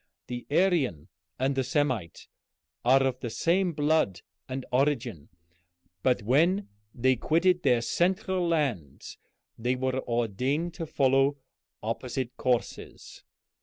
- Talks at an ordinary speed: No, slow, 115 wpm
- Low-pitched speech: Yes, low, 130 Hz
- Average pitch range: Yes, average, 4.6 semitones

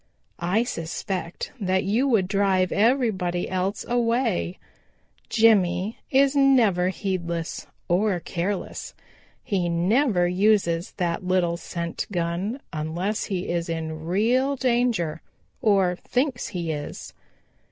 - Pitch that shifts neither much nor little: Yes, average, 4.6 semitones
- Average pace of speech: No, slow, 110 wpm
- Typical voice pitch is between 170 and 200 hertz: Yes, medium, 185 Hz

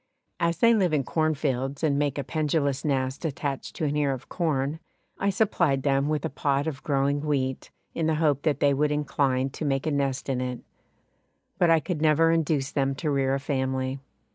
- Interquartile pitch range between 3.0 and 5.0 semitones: No, narrow, 2.5 semitones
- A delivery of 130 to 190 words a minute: No, average, 200 wpm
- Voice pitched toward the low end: No, medium, 145 Hz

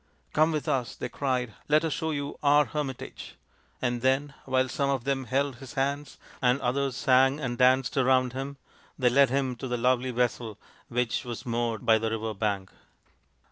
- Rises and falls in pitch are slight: Yes, narrow, 2.3 semitones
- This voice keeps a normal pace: Yes, average, 195 wpm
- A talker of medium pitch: No, low, 130 Hz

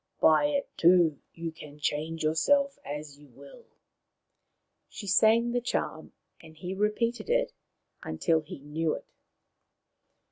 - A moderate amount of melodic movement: No, wide, 7.2 semitones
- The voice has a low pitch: No, medium, 165 Hz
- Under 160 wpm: Yes, slow, 135 wpm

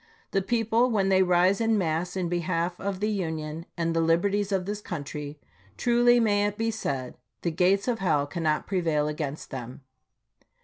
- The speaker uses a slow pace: No, average, 180 wpm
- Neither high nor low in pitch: Yes, medium, 180 Hz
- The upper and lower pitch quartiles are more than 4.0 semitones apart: Yes, average, 4.4 semitones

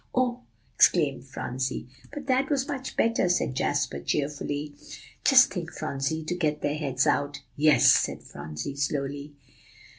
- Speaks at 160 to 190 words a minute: No, average, 140 wpm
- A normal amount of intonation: Yes, average, 4.5 semitones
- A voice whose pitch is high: No, medium, 145 Hz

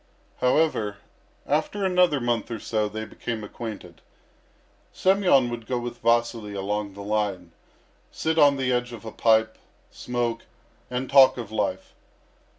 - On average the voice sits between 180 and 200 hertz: No, low, 120 Hz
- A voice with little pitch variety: No, average, 3.5 semitones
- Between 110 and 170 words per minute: Yes, average, 140 wpm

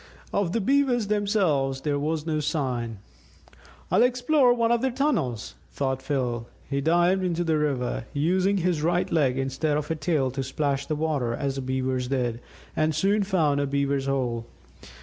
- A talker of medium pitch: Yes, medium, 150 Hz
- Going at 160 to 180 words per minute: Yes, average, 170 wpm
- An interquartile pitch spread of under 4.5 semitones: No, wide, 5.4 semitones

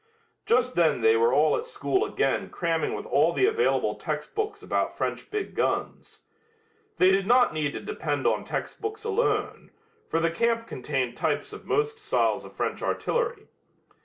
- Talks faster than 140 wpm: Yes, average, 160 wpm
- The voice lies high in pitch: Yes, high, 245 Hz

